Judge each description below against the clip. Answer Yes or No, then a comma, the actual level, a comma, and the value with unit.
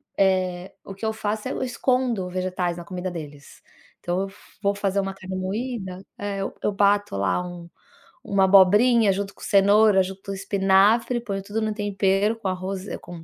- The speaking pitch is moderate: No, high, 195 Hz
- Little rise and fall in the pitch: Yes, narrow, 1.9 semitones